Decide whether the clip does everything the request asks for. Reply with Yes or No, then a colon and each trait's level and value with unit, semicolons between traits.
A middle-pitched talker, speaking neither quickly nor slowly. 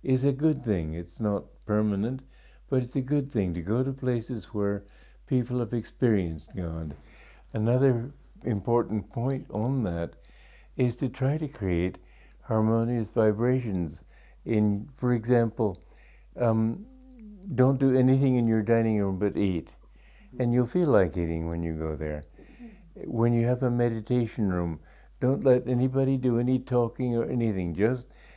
No: low, 115 Hz; average, 150 wpm